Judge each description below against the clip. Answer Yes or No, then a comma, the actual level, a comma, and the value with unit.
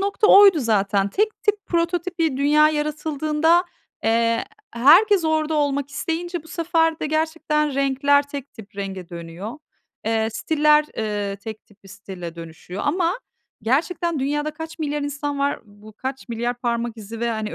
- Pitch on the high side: Yes, very high, 285 Hz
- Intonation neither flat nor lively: No, wide, 6.3 semitones